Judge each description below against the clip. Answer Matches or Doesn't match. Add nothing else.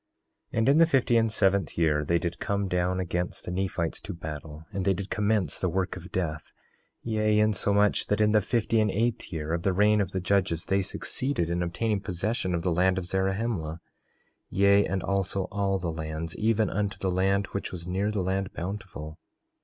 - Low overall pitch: Matches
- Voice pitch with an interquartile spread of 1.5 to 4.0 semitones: Matches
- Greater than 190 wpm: Matches